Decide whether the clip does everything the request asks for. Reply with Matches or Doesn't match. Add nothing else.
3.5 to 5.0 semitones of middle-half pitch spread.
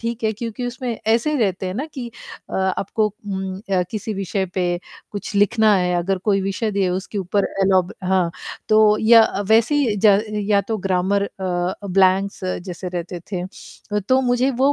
Doesn't match